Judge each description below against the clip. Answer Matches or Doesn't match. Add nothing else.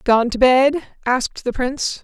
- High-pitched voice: Matches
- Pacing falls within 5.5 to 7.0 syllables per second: Doesn't match